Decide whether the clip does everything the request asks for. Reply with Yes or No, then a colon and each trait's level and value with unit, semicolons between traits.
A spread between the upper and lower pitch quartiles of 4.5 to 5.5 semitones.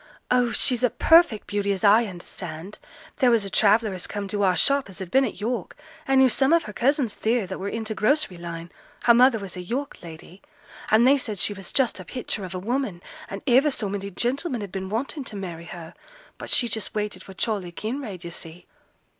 Yes: average, 4.8 semitones